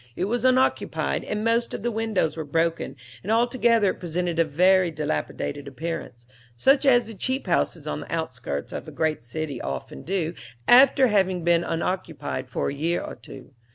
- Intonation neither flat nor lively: No, wide, 6.5 semitones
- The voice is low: No, medium, 175 Hz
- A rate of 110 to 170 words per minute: No, average, 180 wpm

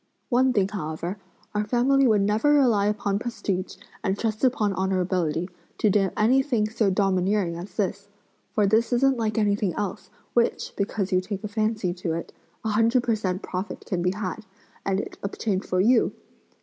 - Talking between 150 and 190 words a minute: Yes, average, 175 wpm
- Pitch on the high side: Yes, high, 205 Hz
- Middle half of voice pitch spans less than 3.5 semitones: Yes, average, 2.9 semitones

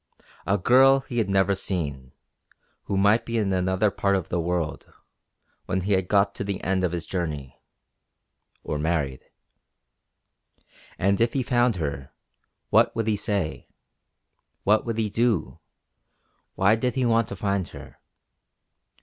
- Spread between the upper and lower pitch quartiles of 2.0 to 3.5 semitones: No, average, 4.3 semitones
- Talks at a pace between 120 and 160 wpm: Yes, average, 150 wpm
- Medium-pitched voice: No, low, 100 Hz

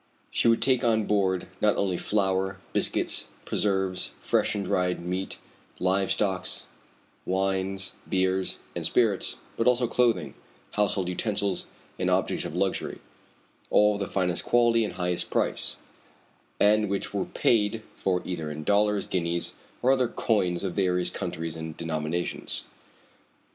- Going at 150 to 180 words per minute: No, average, 140 wpm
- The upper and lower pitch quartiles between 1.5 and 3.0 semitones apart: Yes, narrow, 2.6 semitones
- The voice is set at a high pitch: No, very low, 95 Hz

